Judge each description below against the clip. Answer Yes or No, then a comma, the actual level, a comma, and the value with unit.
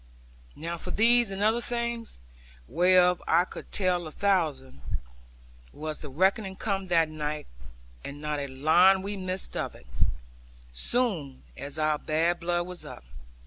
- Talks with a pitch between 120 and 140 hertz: No, medium, 175 Hz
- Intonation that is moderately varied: Yes, average, 4.2 semitones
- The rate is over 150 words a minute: No, average, 145 wpm